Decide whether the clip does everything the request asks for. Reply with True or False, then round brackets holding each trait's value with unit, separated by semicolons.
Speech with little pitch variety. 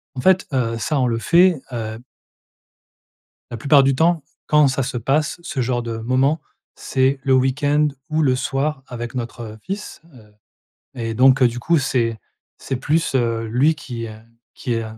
False (3.7 semitones)